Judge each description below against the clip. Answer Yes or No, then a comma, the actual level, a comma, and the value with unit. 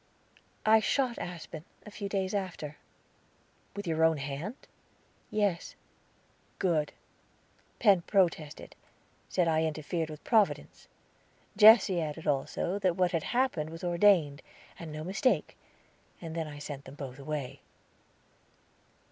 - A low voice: No, medium, 170 Hz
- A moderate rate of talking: No, slow, 120 wpm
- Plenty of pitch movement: No, average, 4.6 semitones